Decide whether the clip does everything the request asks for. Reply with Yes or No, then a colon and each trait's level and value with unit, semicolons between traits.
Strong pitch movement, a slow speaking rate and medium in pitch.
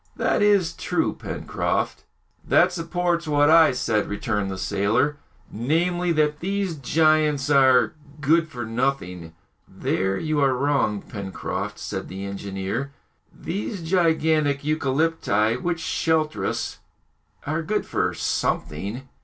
Yes: wide, 6.7 semitones; slow, 120 wpm; medium, 145 Hz